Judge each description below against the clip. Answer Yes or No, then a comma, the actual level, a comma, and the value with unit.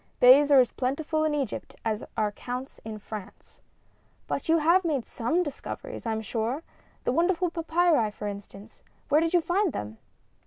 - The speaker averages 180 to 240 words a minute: No, average, 170 wpm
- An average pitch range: No, wide, 6.9 semitones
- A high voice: Yes, very high, 275 Hz